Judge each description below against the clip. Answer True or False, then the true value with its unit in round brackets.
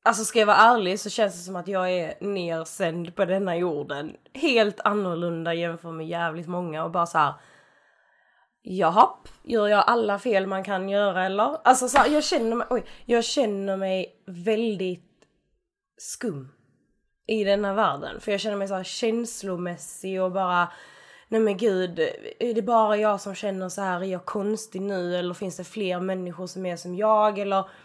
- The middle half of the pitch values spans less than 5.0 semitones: True (3.6 semitones)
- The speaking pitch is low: False (195 Hz)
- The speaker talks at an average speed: True (180 wpm)